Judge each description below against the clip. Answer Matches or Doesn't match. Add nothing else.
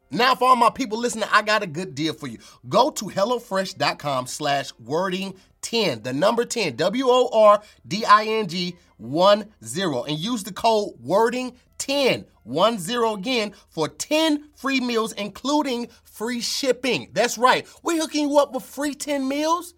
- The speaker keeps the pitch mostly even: Doesn't match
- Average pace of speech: Matches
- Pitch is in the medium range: Doesn't match